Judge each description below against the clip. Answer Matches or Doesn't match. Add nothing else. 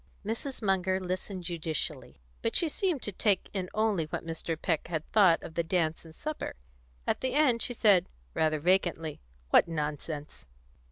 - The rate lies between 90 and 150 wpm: Doesn't match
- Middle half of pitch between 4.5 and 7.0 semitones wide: Matches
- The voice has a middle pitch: Matches